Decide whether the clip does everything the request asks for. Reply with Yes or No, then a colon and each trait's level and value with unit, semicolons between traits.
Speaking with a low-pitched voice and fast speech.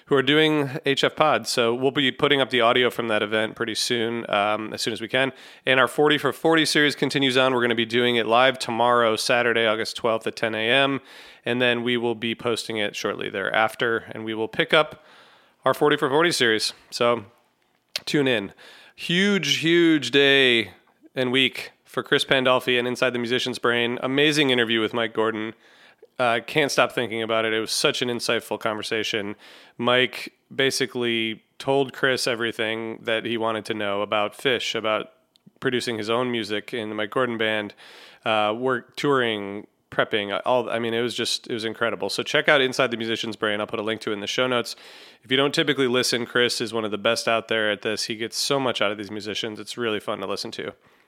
Yes: low, 120 Hz; fast, 210 wpm